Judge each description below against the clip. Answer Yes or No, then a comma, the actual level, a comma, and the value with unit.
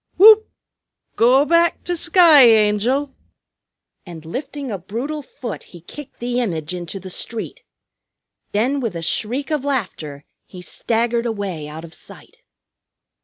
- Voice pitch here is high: Yes, high, 235 Hz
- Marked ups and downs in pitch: Yes, wide, 7.5 semitones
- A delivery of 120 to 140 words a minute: Yes, slow, 135 wpm